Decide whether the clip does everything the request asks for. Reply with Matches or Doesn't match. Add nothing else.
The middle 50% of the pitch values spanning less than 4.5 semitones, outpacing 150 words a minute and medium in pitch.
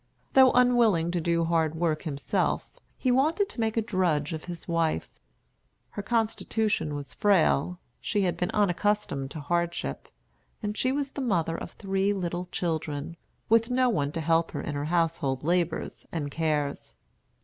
Doesn't match